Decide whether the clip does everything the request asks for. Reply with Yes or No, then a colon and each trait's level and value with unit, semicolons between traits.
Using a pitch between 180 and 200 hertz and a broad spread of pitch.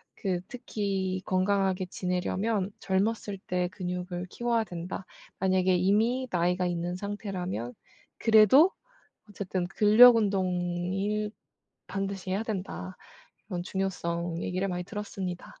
No: high, 190 Hz; narrow, 2.4 semitones